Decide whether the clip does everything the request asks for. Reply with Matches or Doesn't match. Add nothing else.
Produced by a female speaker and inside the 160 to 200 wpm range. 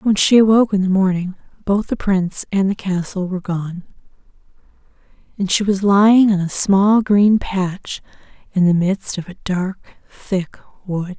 Matches